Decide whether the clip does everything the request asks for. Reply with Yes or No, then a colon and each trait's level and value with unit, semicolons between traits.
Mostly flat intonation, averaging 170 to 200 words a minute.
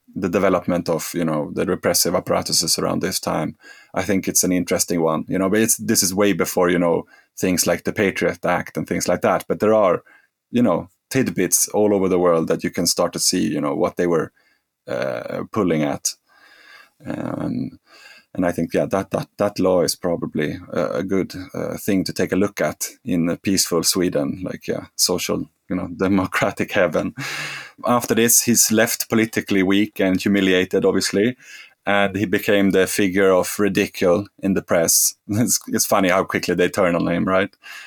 Yes: narrow, 2.2 semitones; average, 190 wpm